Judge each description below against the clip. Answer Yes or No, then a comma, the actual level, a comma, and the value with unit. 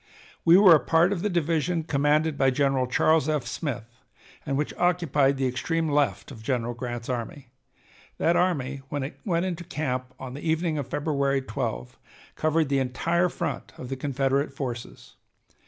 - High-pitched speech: No, medium, 140 Hz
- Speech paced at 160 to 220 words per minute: Yes, average, 170 wpm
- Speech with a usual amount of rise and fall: Yes, average, 4.0 semitones